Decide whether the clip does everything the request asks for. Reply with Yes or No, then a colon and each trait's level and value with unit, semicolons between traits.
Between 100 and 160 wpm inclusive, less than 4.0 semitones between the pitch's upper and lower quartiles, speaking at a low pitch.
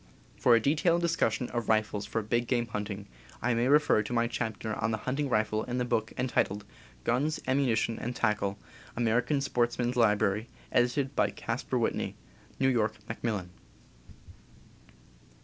Yes: average, 150 wpm; average, 2.7 semitones; low, 120 Hz